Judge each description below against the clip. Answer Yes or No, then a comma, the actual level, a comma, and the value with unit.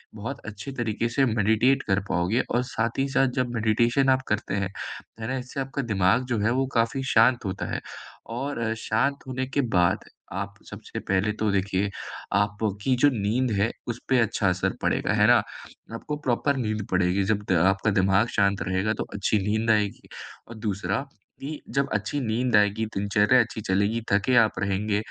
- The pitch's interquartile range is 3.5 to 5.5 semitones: Yes, average, 3.8 semitones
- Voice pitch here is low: Yes, low, 110 Hz